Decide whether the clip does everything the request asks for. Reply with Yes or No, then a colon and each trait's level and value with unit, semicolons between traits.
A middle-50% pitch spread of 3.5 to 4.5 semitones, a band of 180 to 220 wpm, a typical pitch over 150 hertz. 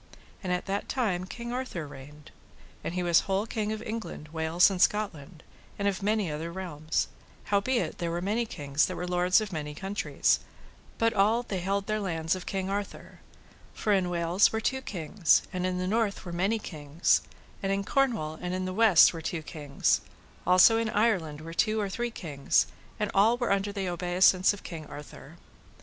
Yes: average, 4.0 semitones; average, 190 wpm; medium, 185 Hz